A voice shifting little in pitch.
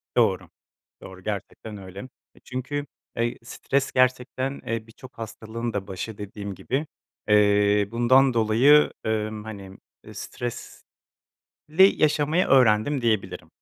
No: average, 3.8 semitones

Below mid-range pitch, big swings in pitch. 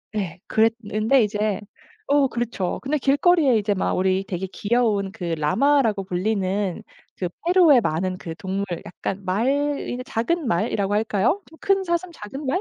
No: high, 215 Hz; wide, 6.4 semitones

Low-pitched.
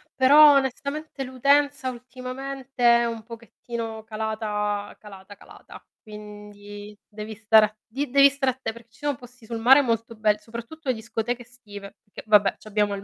No: high, 230 Hz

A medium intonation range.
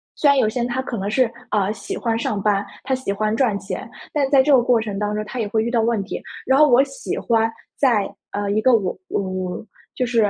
Yes: average, 3.7 semitones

